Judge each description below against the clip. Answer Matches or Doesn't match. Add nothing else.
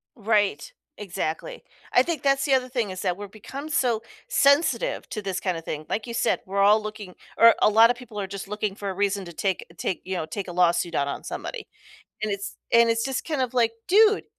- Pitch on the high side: Matches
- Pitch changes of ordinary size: Matches